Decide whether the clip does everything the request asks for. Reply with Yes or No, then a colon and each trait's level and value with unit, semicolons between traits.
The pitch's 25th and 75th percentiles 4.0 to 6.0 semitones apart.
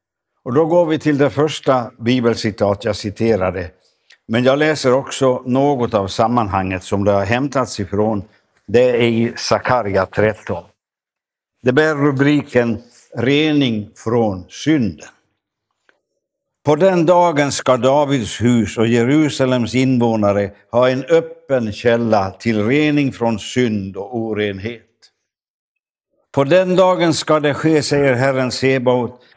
Yes: average, 4.5 semitones